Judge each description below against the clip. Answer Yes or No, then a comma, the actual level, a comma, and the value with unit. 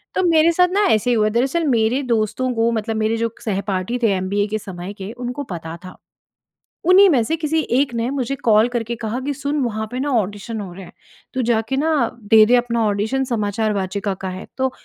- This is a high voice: Yes, high, 230 Hz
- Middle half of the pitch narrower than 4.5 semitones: Yes, average, 4.1 semitones